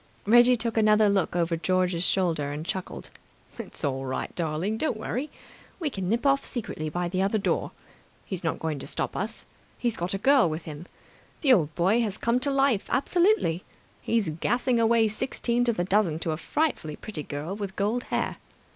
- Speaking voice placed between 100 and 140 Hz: No, high, 200 Hz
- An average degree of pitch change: No, wide, 6.0 semitones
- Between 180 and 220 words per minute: Yes, average, 190 wpm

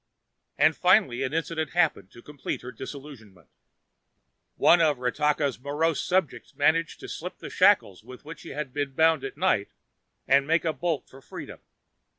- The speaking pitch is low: No, medium, 145 Hz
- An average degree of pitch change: Yes, average, 4.0 semitones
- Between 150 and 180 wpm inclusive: Yes, average, 160 wpm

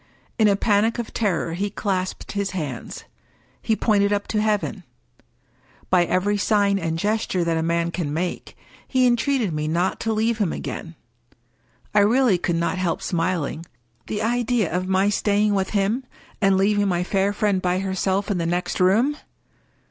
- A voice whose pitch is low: No, high, 195 Hz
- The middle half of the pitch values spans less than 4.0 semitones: Yes, average, 3.0 semitones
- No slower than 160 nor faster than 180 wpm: Yes, average, 170 wpm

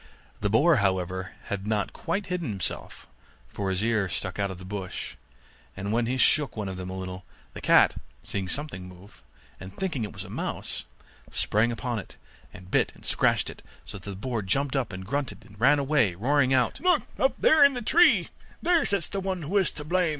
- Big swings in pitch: Yes, wide, 7.6 semitones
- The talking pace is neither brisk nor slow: No, fast, 210 wpm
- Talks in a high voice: No, low, 110 Hz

